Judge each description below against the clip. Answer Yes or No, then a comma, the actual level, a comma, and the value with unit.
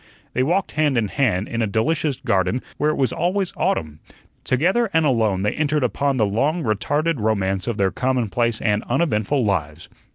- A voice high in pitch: No, low, 125 Hz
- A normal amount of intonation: No, wide, 6.4 semitones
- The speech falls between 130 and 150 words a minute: No, average, 175 wpm